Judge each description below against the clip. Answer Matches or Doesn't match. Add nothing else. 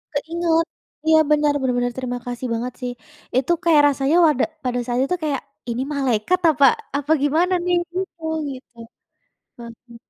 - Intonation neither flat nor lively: Matches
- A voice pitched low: Doesn't match